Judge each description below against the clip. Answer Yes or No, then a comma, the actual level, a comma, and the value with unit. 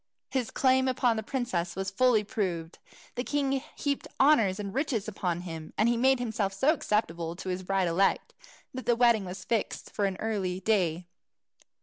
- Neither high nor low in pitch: No, high, 210 Hz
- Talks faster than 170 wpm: Yes, average, 180 wpm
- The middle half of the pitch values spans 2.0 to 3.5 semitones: No, average, 5.0 semitones